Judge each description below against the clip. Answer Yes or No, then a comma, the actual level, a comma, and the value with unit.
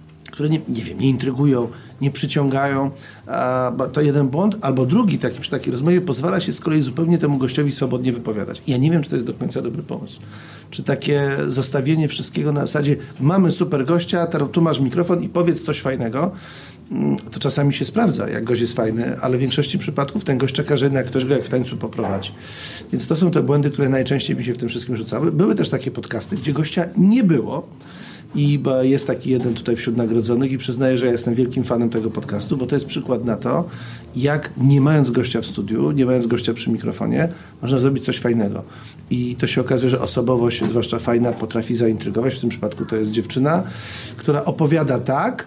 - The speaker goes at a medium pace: No, fast, 200 wpm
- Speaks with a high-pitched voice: No, low, 135 Hz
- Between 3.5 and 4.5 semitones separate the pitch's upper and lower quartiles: Yes, average, 3.8 semitones